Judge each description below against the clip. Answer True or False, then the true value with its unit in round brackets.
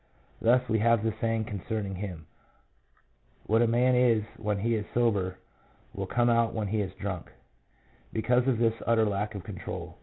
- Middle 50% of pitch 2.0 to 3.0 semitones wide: True (2.6 semitones)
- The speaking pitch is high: False (110 Hz)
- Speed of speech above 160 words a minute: True (180 wpm)